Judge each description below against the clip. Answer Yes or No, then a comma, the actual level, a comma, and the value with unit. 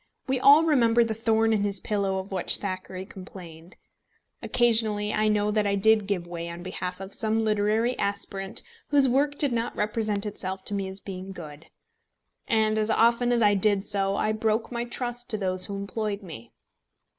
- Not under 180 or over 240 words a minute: Yes, average, 185 wpm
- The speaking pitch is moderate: No, high, 210 Hz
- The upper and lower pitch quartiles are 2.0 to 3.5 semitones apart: Yes, average, 2.8 semitones